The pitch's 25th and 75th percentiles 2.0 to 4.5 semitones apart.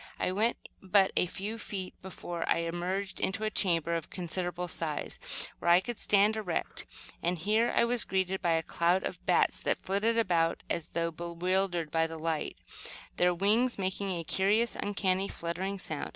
Yes: average, 2.9 semitones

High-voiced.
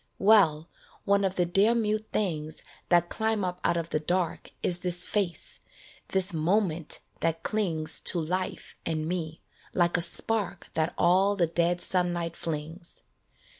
No: medium, 175 Hz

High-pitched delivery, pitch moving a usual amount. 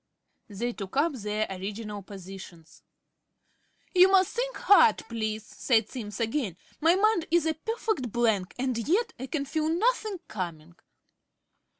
No: high, 240 Hz; wide, 8.4 semitones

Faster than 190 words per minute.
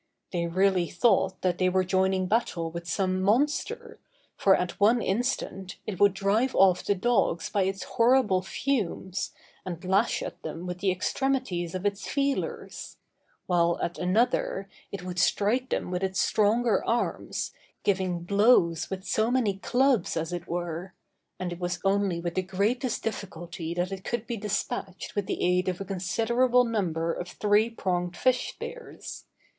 No: average, 160 wpm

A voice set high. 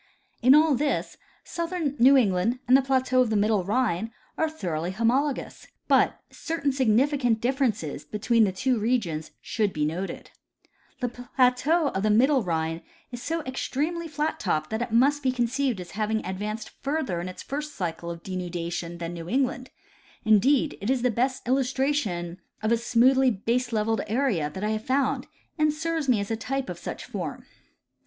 Yes: high, 240 Hz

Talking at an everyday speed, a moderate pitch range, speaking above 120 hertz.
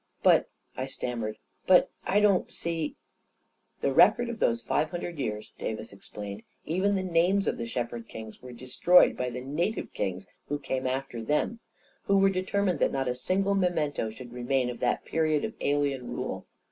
No: average, 190 wpm; wide, 7.0 semitones; medium, 140 Hz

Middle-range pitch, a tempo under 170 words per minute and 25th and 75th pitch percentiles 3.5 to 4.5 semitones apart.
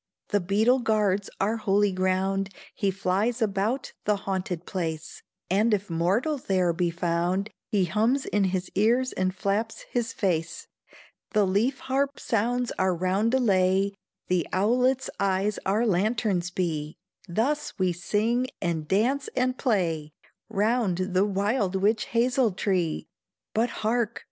No: high, 200 Hz; slow, 135 wpm; average, 3.8 semitones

